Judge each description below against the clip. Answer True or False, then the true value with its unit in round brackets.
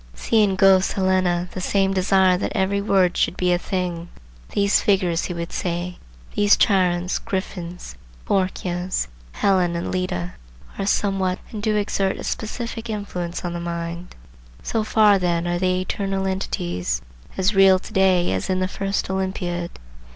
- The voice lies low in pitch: False (185 Hz)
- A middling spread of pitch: False (1.8 semitones)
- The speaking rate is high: False (160 wpm)